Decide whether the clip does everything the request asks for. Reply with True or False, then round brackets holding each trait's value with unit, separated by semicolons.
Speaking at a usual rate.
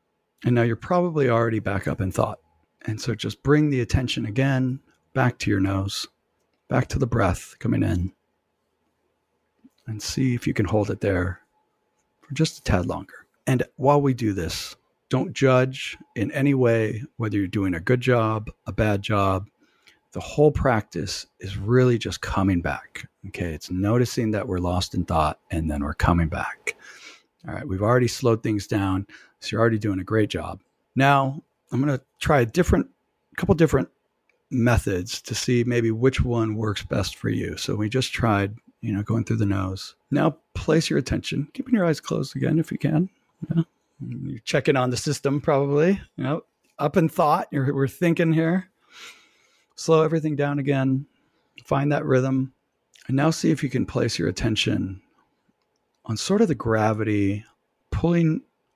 True (175 wpm)